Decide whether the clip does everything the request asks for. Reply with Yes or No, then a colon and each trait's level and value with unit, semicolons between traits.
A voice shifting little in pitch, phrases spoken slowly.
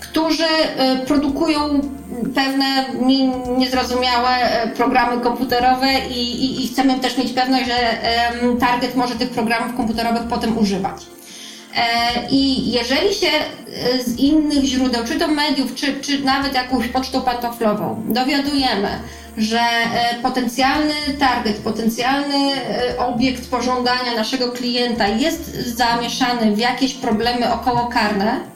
Yes: narrow, 2.1 semitones; slow, 105 wpm